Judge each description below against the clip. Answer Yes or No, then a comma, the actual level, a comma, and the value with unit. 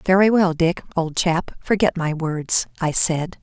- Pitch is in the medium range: Yes, medium, 170 Hz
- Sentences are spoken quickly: No, average, 175 wpm